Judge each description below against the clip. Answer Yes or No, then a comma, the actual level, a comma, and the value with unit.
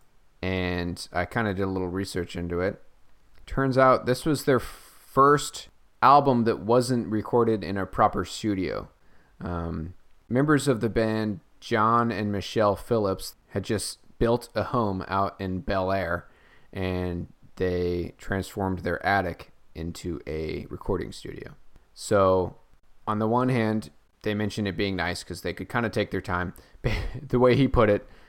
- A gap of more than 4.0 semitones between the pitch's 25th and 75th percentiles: Yes, average, 4.6 semitones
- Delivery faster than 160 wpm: No, average, 155 wpm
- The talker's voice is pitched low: Yes, low, 100 Hz